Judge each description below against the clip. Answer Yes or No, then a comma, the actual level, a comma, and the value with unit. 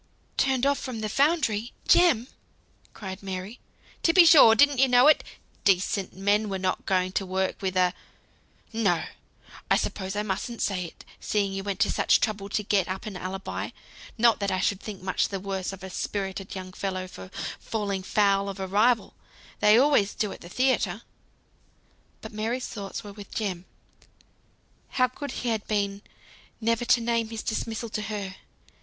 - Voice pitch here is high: Yes, high, 205 Hz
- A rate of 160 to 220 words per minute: Yes, average, 175 wpm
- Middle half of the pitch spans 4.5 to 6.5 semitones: No, average, 3.3 semitones